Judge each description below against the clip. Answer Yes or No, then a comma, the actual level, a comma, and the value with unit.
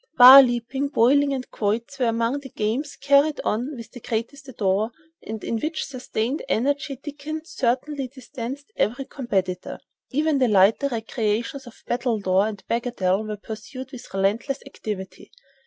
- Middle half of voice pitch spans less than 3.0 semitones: No, average, 4.1 semitones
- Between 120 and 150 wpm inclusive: Yes, average, 140 wpm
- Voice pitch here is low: No, high, 245 Hz